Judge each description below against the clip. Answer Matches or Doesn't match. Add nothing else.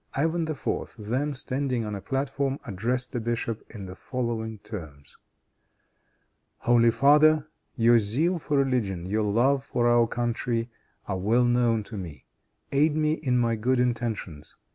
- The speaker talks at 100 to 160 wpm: Matches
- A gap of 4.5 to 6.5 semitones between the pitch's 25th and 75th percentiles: Doesn't match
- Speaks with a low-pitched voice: Matches